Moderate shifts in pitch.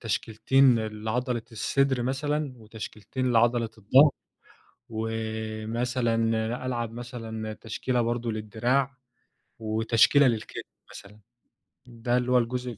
No: narrow, 2.1 semitones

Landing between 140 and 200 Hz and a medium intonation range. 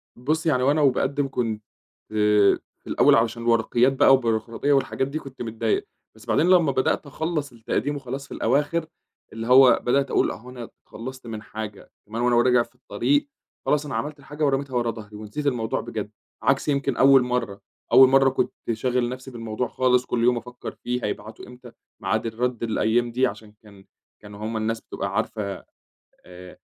No: low, 125 Hz; average, 3.4 semitones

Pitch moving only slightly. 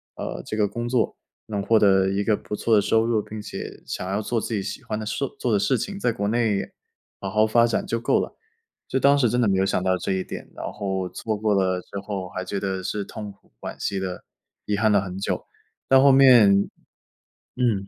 No: average, 3.0 semitones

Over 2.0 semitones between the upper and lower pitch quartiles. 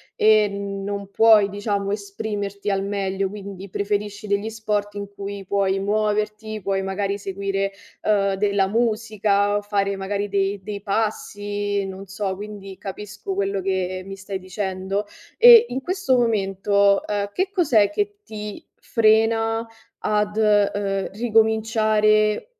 No: narrow, 1.4 semitones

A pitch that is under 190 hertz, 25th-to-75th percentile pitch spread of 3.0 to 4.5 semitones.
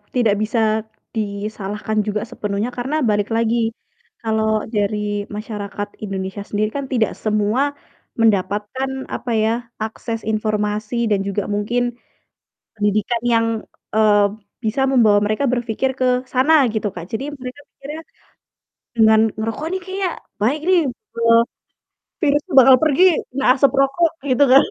No: high, 220 Hz; average, 3.9 semitones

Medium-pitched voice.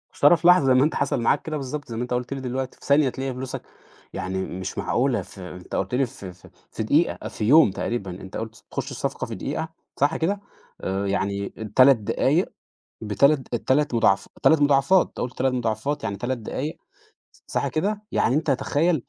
No: low, 130 Hz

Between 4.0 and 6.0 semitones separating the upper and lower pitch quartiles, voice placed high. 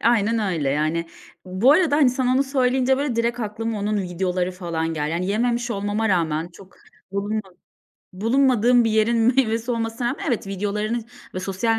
Yes: average, 4.6 semitones; high, 220 Hz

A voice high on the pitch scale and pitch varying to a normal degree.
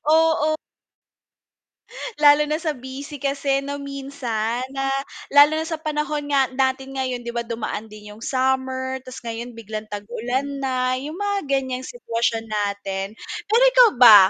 Yes: very high, 265 Hz; average, 3.5 semitones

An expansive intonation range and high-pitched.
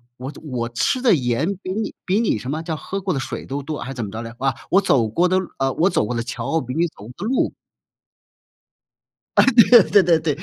No: wide, 7.1 semitones; medium, 150 Hz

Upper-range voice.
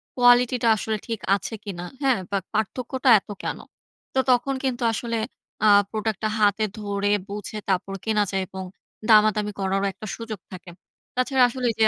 Yes: high, 215 Hz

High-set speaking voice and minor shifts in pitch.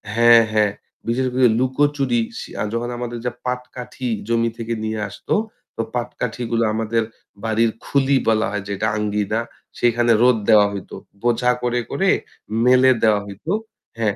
No: low, 115 Hz; narrow, 2.2 semitones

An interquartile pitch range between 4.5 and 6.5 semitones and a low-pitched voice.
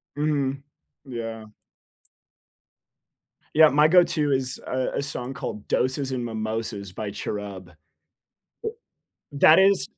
Yes: average, 5.0 semitones; low, 130 Hz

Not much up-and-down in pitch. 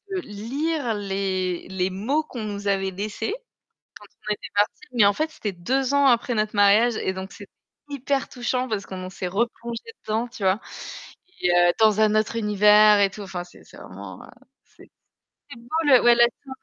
No: average, 3.7 semitones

